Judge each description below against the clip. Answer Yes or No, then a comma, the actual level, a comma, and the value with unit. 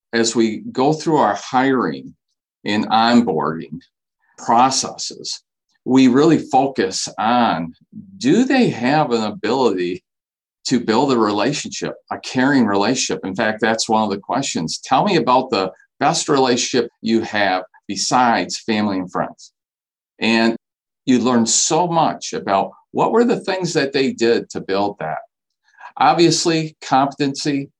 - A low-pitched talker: Yes, low, 125 Hz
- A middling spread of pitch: No, wide, 6.0 semitones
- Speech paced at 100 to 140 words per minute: Yes, slow, 135 wpm